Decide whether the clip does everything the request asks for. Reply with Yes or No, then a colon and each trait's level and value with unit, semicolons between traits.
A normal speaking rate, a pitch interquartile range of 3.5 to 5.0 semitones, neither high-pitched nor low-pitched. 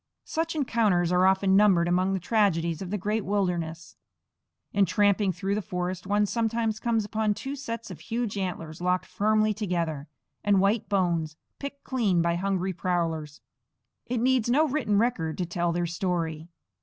No: average, 165 wpm; average, 3.9 semitones; high, 195 Hz